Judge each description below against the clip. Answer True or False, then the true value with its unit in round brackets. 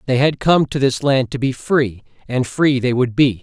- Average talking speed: False (245 wpm)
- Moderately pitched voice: False (130 Hz)